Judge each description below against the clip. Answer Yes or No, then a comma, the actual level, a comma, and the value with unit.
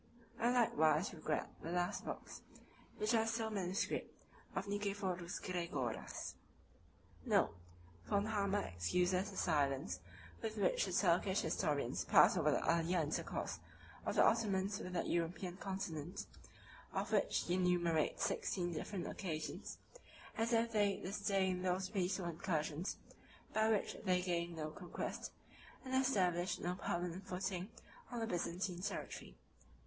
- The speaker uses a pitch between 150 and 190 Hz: Yes, medium, 185 Hz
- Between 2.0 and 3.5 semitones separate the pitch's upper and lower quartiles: Yes, average, 2.9 semitones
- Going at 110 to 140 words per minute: Yes, slow, 135 wpm